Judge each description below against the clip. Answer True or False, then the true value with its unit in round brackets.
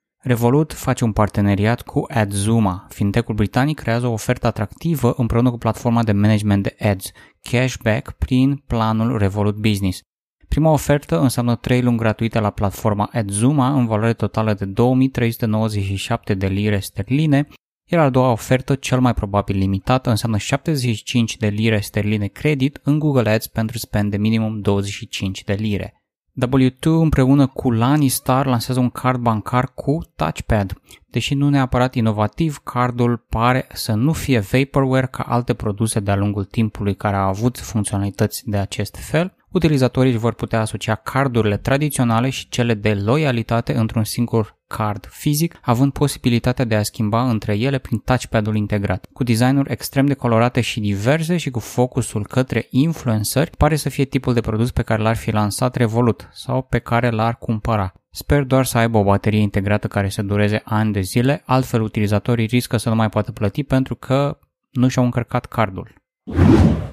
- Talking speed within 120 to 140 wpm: False (160 wpm)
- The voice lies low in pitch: True (115 Hz)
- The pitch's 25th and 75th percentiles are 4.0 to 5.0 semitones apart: False (3.5 semitones)